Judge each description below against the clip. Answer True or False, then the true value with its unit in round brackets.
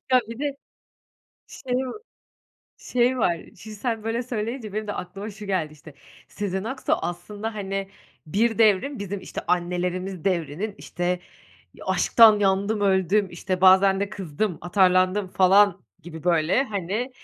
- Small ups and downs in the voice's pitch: False (3.2 semitones)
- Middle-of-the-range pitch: False (195 Hz)